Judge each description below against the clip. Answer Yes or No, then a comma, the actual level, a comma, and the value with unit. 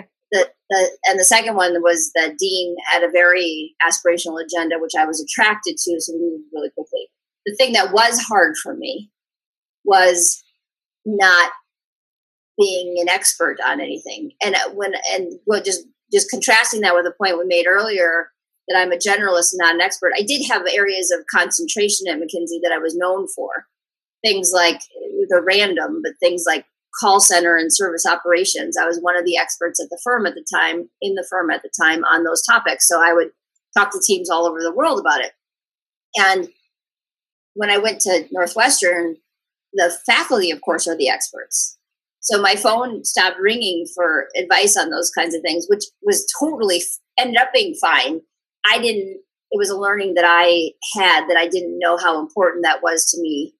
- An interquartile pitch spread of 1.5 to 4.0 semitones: Yes, average, 3.6 semitones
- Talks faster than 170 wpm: Yes, average, 190 wpm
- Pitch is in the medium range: Yes, medium, 180 Hz